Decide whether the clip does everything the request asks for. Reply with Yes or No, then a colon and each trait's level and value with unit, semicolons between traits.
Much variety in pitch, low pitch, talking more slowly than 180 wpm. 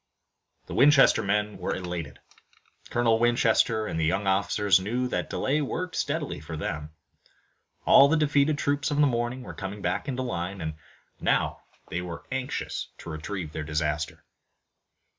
Yes: wide, 7.3 semitones; low, 105 Hz; average, 155 wpm